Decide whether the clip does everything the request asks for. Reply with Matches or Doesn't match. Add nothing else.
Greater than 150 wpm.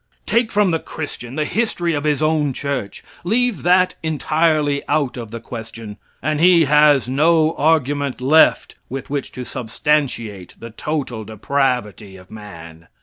Doesn't match